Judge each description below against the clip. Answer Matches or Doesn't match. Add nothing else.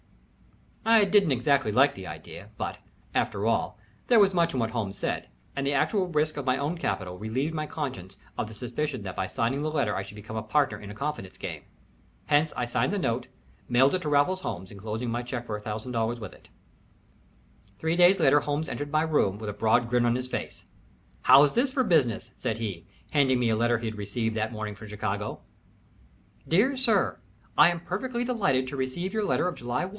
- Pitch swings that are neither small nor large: Doesn't match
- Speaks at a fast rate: Matches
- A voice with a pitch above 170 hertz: Doesn't match